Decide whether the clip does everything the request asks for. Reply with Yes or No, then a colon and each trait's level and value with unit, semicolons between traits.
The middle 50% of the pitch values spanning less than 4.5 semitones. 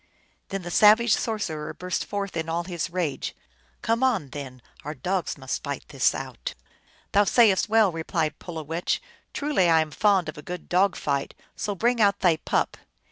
No: average, 4.9 semitones